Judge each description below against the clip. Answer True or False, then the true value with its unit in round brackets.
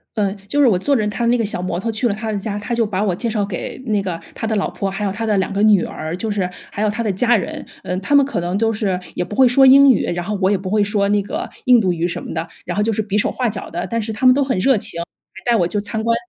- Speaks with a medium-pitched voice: False (210 Hz)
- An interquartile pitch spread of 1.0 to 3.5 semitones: True (3.2 semitones)